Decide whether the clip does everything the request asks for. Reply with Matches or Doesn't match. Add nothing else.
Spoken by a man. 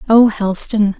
Doesn't match